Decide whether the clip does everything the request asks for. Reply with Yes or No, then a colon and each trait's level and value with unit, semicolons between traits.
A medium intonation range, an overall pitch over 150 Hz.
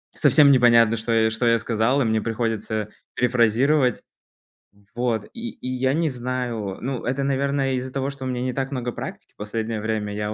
No: average, 3.0 semitones; low, 120 Hz